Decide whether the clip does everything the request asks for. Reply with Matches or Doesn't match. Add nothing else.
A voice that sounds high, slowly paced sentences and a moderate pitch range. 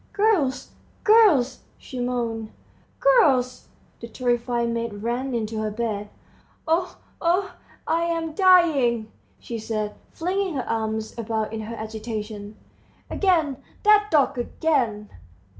Doesn't match